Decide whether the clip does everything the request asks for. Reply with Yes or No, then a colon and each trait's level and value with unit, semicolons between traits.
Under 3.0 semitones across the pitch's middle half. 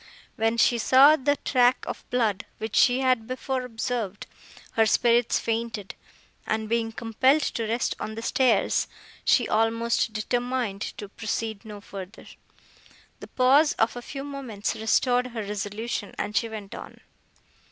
Yes: narrow, 2.5 semitones